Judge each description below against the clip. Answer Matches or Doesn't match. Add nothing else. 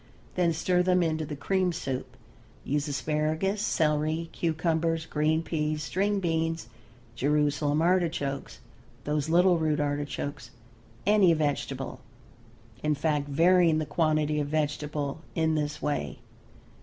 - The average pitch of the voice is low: Doesn't match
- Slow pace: Matches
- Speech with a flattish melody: Matches